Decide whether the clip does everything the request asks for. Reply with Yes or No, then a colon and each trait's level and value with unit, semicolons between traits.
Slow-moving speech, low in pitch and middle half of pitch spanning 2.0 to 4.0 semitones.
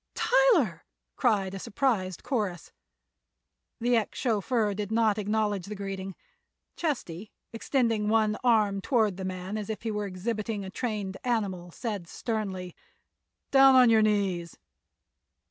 No: slow, 130 wpm; high, 210 Hz; average, 3.0 semitones